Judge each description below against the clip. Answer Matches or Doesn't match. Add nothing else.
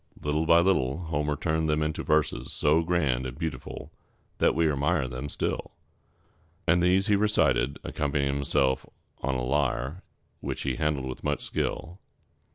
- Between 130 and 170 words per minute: Matches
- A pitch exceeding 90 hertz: Doesn't match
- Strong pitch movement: Doesn't match